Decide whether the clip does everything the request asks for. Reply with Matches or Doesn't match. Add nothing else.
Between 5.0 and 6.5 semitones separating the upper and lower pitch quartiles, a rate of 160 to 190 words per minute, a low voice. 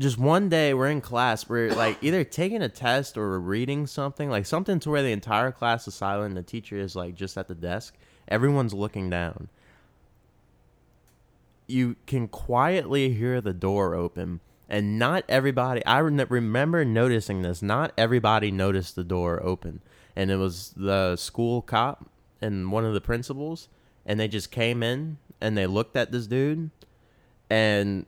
Matches